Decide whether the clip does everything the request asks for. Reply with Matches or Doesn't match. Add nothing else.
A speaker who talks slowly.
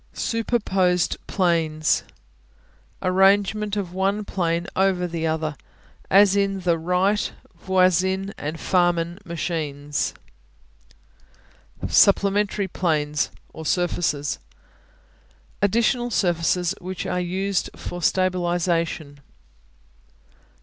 Matches